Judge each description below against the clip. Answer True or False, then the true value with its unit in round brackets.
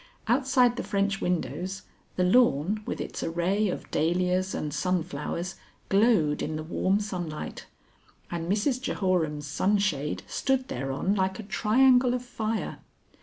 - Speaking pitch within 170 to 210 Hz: True (190 Hz)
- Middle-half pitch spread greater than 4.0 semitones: True (4.7 semitones)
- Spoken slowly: True (130 wpm)